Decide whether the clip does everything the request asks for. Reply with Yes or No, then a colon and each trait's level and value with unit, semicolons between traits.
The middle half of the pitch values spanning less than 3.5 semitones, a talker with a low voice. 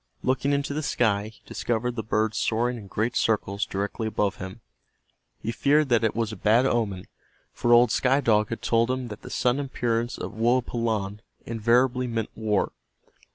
Yes: narrow, 2.4 semitones; low, 115 Hz